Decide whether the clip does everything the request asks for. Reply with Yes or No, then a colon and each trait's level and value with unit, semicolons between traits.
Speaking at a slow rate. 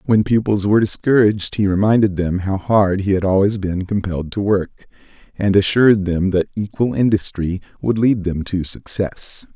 No: average, 170 wpm